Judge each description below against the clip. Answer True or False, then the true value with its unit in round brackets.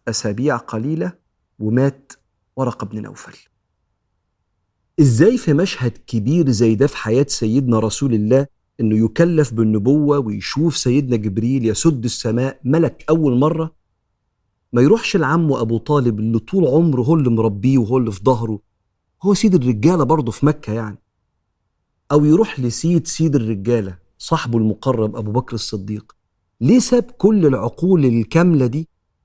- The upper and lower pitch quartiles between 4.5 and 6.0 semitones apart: True (5.6 semitones)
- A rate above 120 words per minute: True (135 wpm)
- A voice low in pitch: True (130 Hz)